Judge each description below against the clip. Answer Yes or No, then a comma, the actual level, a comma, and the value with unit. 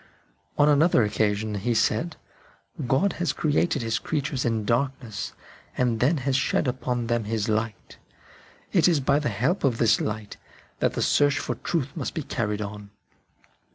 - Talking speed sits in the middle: Yes, average, 165 wpm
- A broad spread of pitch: No, average, 4.9 semitones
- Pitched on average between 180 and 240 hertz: No, low, 125 Hz